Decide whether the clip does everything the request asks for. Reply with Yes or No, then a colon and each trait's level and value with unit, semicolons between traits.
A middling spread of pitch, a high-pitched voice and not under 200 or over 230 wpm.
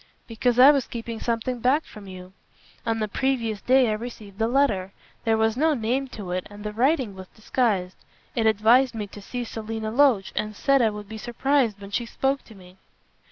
Yes: average, 3.4 semitones; high, 225 Hz; fast, 205 wpm